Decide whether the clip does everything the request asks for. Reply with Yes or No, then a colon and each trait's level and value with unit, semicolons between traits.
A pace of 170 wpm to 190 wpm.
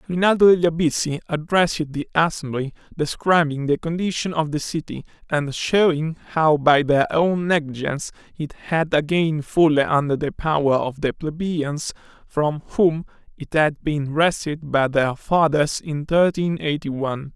No: average, 145 wpm